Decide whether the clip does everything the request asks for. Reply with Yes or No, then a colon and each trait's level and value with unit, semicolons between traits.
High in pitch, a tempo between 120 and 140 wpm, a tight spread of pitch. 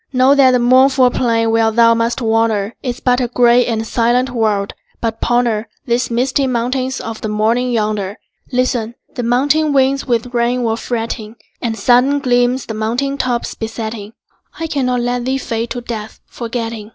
No: high, 240 Hz; average, 170 wpm; narrow, 2.0 semitones